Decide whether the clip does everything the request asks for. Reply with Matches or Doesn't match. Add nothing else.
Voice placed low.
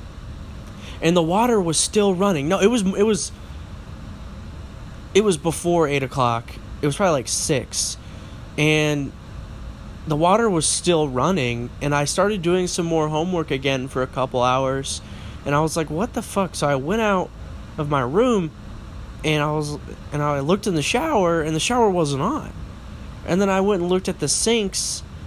Doesn't match